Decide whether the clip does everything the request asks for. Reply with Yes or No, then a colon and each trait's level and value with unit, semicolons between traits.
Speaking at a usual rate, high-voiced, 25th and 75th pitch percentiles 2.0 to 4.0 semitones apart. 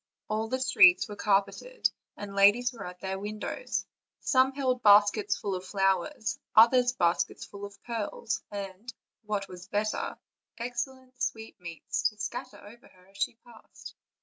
Yes: average, 150 wpm; high, 210 Hz; average, 3.3 semitones